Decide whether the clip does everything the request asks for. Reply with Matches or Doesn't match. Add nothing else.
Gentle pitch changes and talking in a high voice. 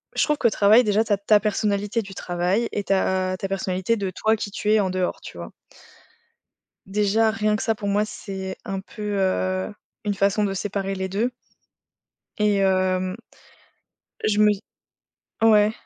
Matches